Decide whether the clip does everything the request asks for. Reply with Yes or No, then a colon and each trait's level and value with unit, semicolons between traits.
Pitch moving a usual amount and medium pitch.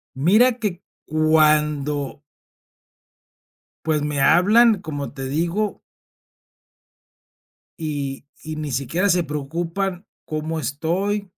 Yes: average, 3.8 semitones; medium, 155 Hz